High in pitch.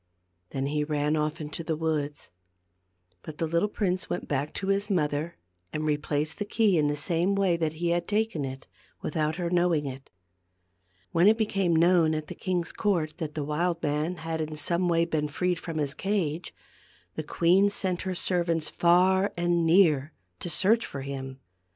No: medium, 165 Hz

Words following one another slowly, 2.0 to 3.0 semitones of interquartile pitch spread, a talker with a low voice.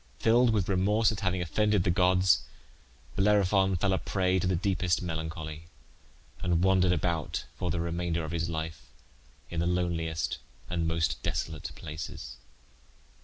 No: average, 145 wpm; narrow, 2.6 semitones; very low, 90 Hz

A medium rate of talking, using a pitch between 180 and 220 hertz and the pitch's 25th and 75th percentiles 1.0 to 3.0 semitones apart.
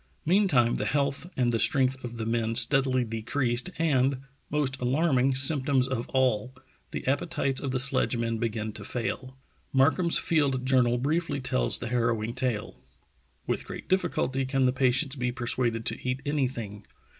No: average, 155 wpm; low, 130 Hz; narrow, 2.6 semitones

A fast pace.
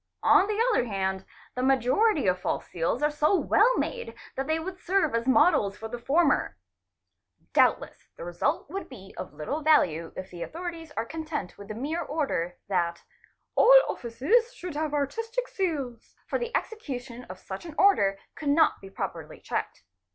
No: average, 180 wpm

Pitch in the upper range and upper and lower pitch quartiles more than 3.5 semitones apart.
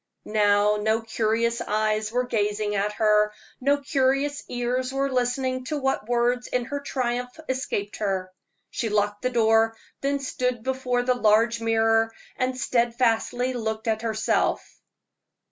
No: high, 235 Hz; average, 2.8 semitones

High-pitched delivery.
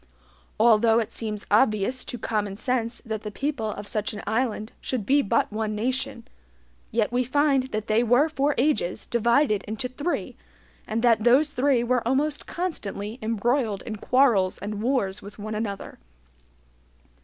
Yes: high, 230 Hz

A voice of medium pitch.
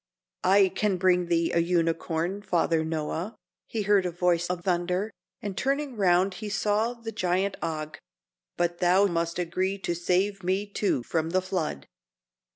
Yes: medium, 180 Hz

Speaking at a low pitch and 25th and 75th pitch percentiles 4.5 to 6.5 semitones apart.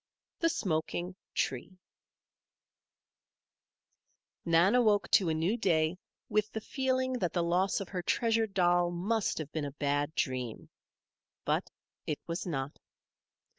No: medium, 175 Hz; average, 5.1 semitones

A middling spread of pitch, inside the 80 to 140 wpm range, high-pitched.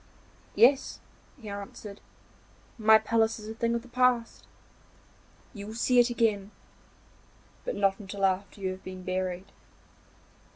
Yes: average, 3.1 semitones; slow, 135 wpm; high, 215 Hz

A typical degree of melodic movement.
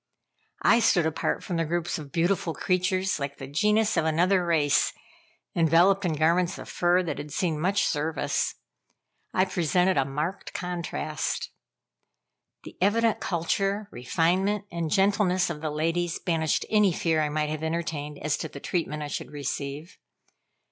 Yes: average, 3.4 semitones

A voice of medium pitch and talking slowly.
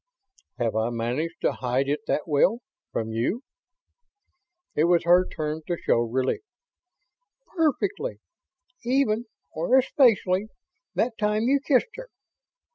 Yes: medium, 180 Hz; slow, 120 wpm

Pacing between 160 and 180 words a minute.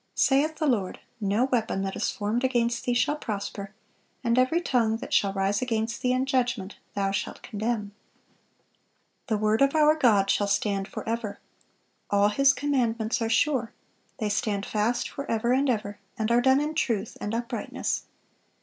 Yes: average, 165 wpm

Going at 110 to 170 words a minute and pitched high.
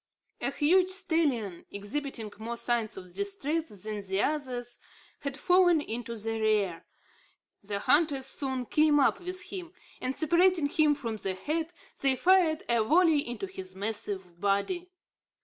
Yes: average, 145 wpm; very high, 265 Hz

